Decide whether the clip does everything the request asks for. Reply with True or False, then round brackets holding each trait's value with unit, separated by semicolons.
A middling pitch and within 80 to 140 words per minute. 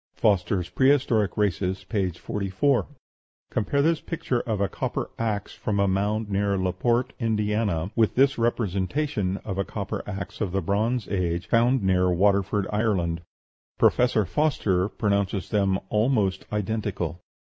False (100 Hz; 135 wpm)